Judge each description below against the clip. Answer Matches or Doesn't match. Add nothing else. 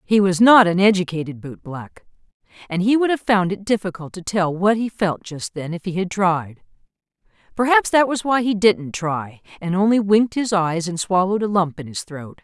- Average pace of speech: Doesn't match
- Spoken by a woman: Matches